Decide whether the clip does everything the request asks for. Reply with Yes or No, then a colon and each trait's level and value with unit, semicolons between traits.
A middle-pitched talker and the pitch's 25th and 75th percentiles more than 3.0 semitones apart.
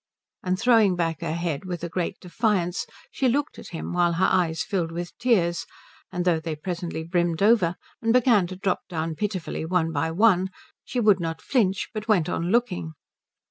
Yes: medium, 180 Hz; average, 3.9 semitones